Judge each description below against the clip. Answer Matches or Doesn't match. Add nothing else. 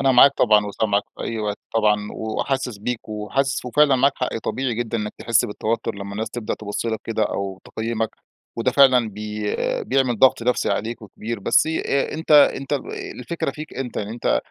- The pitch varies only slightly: Doesn't match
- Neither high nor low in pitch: Doesn't match